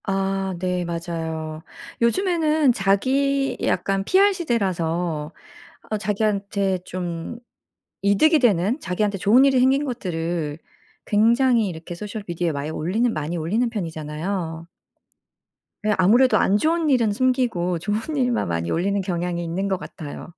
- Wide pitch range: Yes, wide, 5.8 semitones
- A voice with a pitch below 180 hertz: No, high, 195 Hz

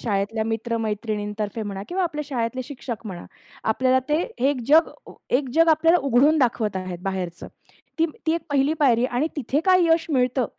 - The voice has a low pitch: No, very high, 250 Hz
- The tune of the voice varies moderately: No, wide, 5.7 semitones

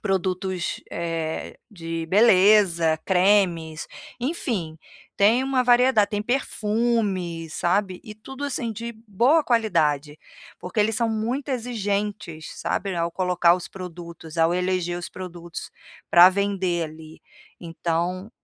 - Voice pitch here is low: No, medium, 185 Hz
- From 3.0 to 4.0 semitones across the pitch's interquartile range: No, average, 4.4 semitones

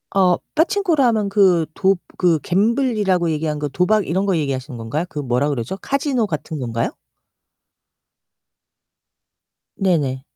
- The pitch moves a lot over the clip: Yes, wide, 6.0 semitones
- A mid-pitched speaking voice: Yes, medium, 180 Hz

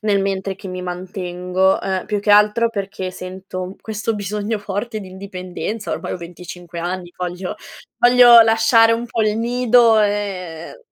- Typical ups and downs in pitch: Yes, average, 3.3 semitones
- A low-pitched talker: No, high, 200 Hz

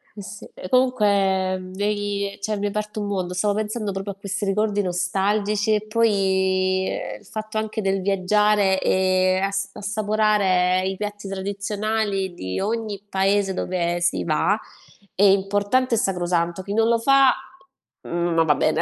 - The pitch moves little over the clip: Yes, narrow, 2.0 semitones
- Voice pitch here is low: No, high, 200 Hz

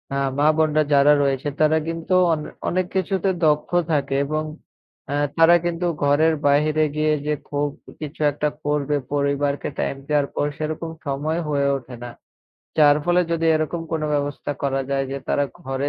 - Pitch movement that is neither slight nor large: No, narrow, 1.8 semitones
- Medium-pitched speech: Yes, medium, 150 Hz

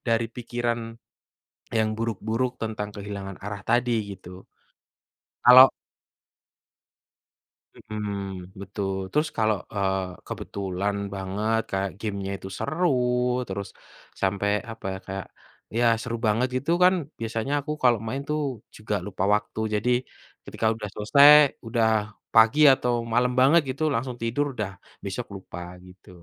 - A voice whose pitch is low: Yes, low, 110 Hz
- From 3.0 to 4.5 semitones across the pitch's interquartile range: Yes, average, 3.5 semitones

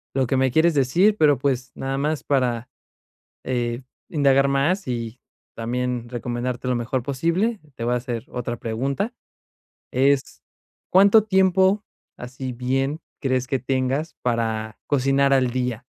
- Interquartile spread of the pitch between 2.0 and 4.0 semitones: Yes, average, 2.8 semitones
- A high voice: No, low, 130 Hz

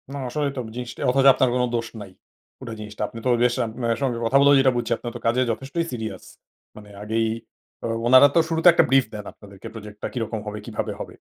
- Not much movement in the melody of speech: No, average, 3.3 semitones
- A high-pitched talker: No, low, 120 Hz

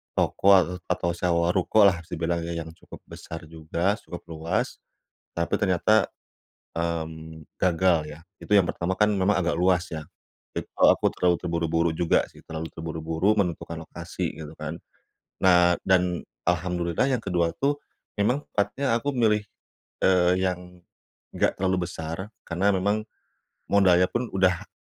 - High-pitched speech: No, very low, 90 Hz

